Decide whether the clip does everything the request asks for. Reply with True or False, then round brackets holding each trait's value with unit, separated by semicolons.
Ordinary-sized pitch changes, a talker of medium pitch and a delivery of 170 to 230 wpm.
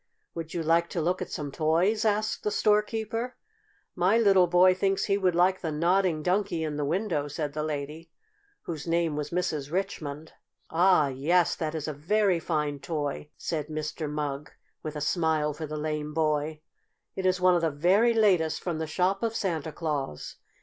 True (3.6 semitones; 165 Hz; 185 wpm)